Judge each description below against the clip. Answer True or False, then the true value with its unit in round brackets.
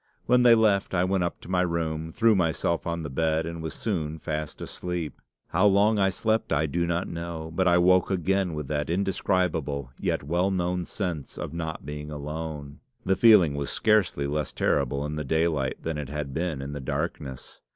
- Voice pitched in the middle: False (85 Hz)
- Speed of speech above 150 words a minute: True (195 wpm)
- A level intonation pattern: False (3.6 semitones)